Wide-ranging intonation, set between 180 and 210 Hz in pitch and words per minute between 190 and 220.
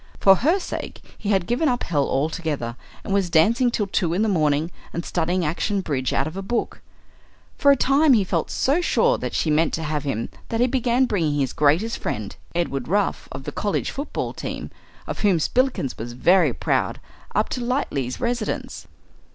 Yes: wide, 7.9 semitones; medium, 185 Hz; average, 195 wpm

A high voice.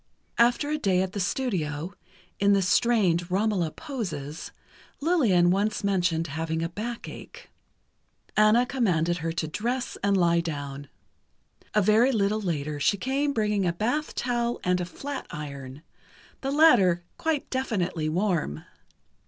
Yes: high, 195 Hz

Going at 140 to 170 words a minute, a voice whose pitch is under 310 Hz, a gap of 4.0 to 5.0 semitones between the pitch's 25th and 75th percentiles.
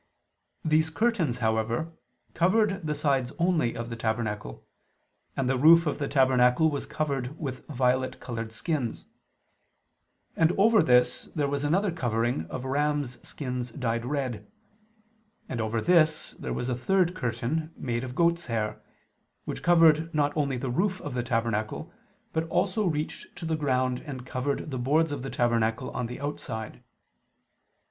Yes: average, 155 wpm; low, 135 Hz; average, 4.7 semitones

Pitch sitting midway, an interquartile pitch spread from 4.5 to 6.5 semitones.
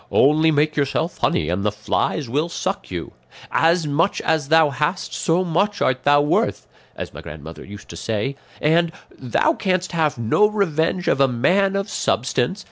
Yes: medium, 155 Hz; wide, 5.6 semitones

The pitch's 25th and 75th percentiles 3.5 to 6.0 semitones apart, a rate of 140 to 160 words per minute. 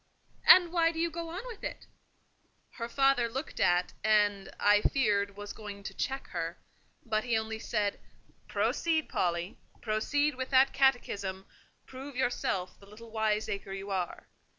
Yes: average, 5.1 semitones; average, 150 wpm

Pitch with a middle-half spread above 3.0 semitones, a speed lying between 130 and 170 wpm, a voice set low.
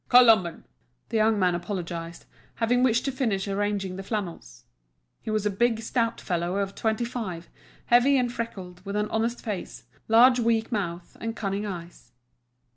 No: average, 4.0 semitones; average, 160 wpm; high, 210 Hz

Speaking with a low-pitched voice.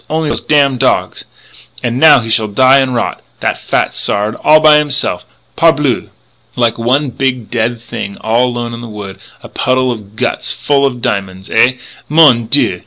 Yes: low, 120 Hz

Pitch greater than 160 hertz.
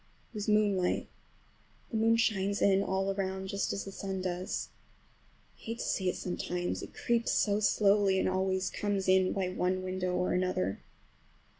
Yes: high, 190 Hz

